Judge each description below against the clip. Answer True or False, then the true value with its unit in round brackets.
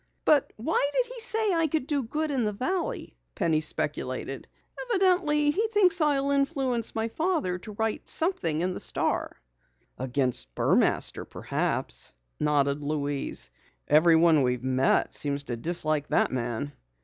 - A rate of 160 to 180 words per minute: False (140 wpm)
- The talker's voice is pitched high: True (220 Hz)